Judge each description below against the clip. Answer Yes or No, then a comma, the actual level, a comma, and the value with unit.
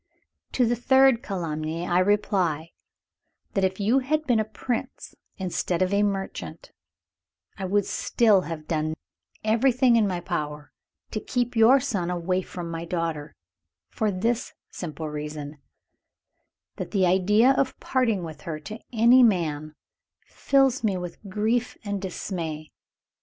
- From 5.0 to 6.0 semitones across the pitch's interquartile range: Yes, wide, 5.6 semitones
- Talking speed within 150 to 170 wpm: No, average, 140 wpm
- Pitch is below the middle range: No, high, 190 Hz